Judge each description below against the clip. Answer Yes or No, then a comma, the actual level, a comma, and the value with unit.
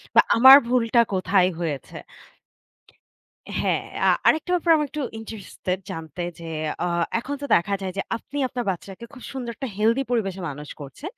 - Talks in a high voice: Yes, high, 225 Hz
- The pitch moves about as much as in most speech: No, wide, 6.4 semitones